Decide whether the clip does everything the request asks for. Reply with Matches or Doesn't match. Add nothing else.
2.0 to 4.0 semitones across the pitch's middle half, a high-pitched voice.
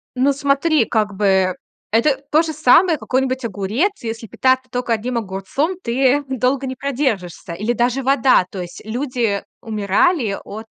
Doesn't match